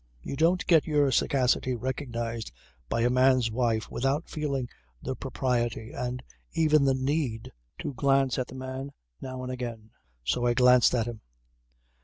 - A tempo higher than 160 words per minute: No, average, 155 wpm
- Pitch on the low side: Yes, low, 130 Hz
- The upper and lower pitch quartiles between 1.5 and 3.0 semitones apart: Yes, narrow, 2.4 semitones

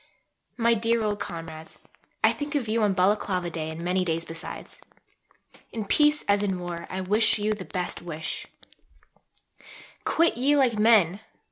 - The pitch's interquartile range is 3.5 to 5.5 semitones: Yes, average, 4.6 semitones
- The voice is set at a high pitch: Yes, high, 205 Hz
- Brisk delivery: No, average, 155 wpm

